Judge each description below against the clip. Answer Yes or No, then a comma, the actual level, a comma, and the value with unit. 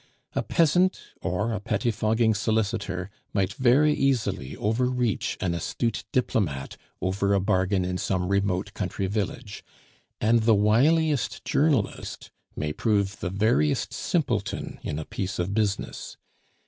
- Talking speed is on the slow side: Yes, slow, 125 wpm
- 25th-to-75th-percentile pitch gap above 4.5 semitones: No, average, 3.8 semitones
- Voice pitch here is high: No, low, 105 Hz